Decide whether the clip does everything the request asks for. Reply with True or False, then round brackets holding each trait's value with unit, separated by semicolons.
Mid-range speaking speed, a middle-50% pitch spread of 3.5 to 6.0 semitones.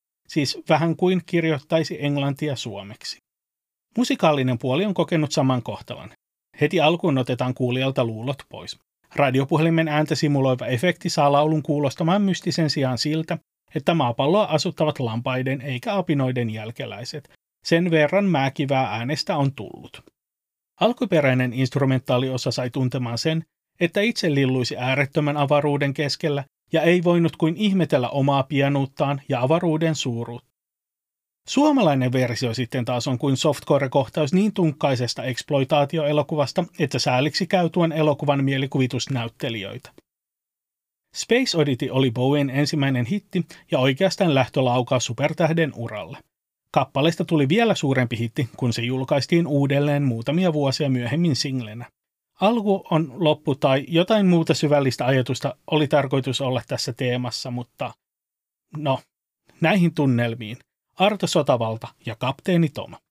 True (115 wpm; 4.0 semitones)